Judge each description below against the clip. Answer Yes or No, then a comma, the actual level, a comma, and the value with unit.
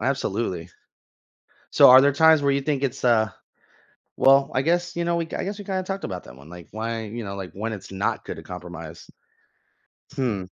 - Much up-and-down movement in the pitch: Yes, wide, 7.4 semitones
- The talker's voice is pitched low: Yes, low, 130 Hz